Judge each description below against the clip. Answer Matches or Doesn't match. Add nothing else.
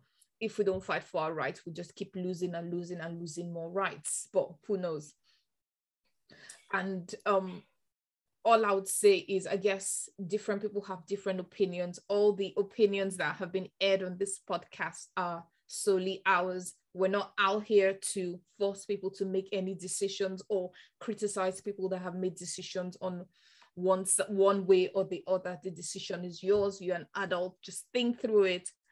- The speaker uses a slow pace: Doesn't match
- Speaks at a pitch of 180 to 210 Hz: Matches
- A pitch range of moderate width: Doesn't match